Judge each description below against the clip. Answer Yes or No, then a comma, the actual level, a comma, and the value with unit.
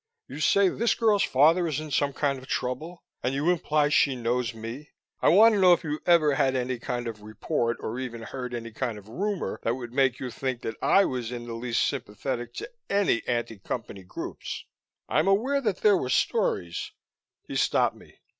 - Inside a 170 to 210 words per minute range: Yes, fast, 205 wpm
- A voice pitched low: Yes, low, 130 Hz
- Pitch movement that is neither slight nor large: No, wide, 5.9 semitones